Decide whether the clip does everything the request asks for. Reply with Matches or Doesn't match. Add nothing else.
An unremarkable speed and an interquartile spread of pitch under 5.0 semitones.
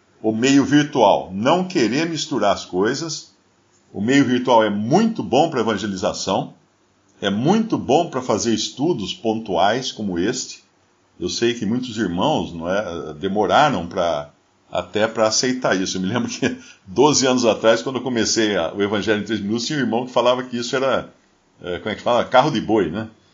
Matches